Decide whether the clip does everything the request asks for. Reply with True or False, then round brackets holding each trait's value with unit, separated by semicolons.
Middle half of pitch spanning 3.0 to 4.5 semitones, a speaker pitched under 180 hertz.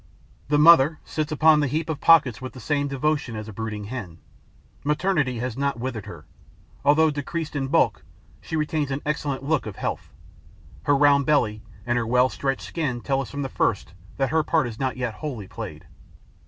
True (3.5 semitones; 140 Hz)